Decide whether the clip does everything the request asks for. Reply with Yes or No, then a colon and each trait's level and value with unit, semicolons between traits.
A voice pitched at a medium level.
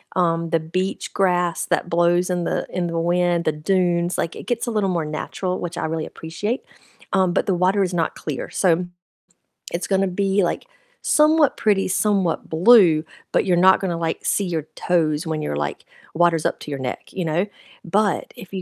Yes: medium, 175 Hz